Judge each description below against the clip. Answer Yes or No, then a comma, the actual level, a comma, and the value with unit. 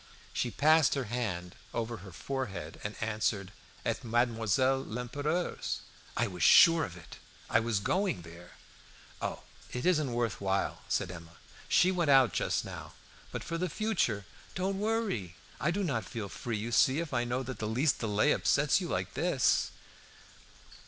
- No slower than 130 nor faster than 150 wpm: No, average, 165 wpm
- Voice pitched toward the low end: Yes, low, 120 Hz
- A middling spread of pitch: No, wide, 6.7 semitones